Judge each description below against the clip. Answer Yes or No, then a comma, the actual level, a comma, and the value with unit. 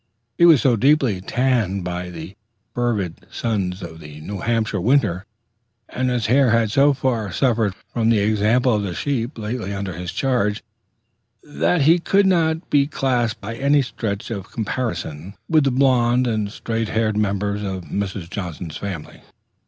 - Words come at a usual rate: Yes, average, 160 wpm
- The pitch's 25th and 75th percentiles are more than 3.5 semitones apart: Yes, average, 4.7 semitones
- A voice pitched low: Yes, low, 110 Hz